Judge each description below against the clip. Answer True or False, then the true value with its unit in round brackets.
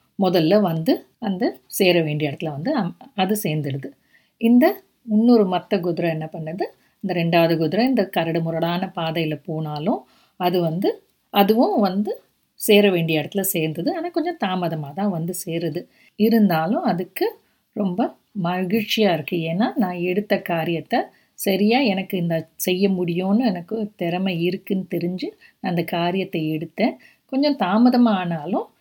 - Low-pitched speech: False (185 Hz)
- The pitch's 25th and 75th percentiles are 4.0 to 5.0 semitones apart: True (4.5 semitones)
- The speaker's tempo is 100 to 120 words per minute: False (130 wpm)